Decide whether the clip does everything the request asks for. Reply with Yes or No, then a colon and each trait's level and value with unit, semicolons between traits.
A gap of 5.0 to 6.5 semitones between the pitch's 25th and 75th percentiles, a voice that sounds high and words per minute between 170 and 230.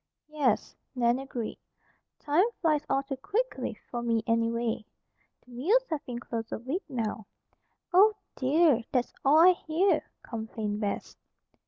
No: wide, 5.6 semitones; very high, 260 Hz; average, 140 wpm